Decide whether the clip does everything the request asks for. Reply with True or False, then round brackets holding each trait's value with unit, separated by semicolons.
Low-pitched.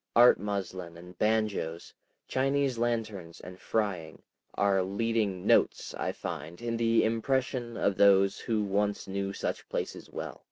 True (100 Hz)